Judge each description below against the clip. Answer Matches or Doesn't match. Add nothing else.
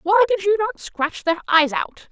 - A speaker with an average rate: Doesn't match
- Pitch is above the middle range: Matches